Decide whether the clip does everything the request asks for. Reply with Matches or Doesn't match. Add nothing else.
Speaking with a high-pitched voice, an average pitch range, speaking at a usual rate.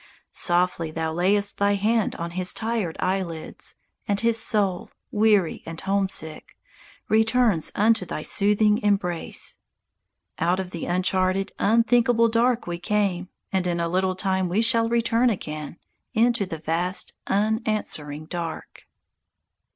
Doesn't match